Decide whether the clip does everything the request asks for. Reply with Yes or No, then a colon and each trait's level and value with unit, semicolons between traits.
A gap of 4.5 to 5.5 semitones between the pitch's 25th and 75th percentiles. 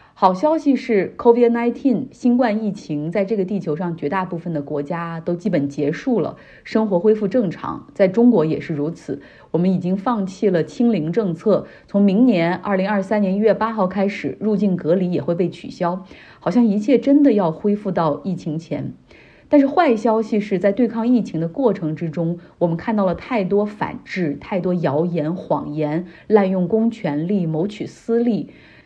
Yes: average, 5.2 semitones